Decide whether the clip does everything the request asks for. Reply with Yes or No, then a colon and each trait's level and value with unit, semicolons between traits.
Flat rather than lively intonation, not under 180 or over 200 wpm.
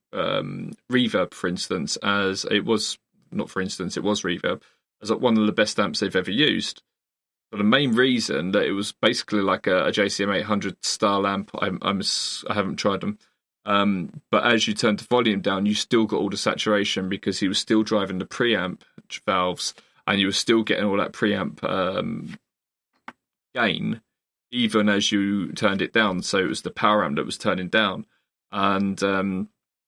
Yes: narrow, 1.9 semitones; average, 185 wpm